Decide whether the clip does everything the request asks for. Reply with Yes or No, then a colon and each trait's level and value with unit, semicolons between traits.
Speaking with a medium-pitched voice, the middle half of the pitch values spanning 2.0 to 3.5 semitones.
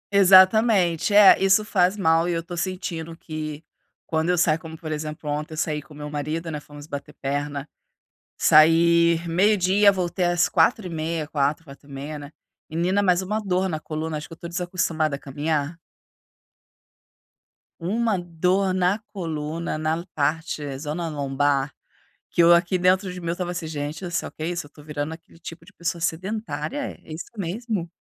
Yes: medium, 165 Hz; average, 3.0 semitones